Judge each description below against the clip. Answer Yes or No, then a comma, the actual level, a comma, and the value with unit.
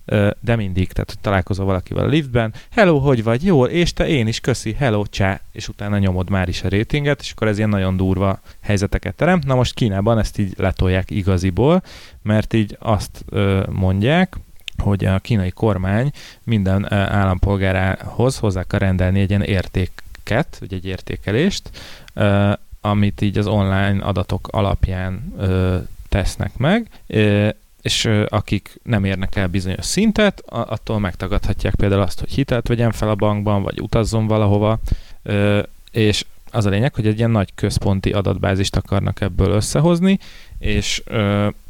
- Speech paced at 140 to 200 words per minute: Yes, average, 145 wpm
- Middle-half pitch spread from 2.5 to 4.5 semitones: Yes, average, 2.9 semitones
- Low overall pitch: Yes, low, 105 Hz